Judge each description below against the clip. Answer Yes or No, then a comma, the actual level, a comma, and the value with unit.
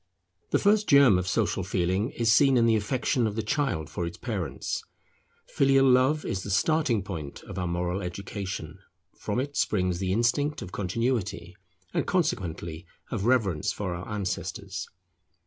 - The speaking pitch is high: No, low, 105 Hz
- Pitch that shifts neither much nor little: No, wide, 5.9 semitones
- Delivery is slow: No, average, 160 wpm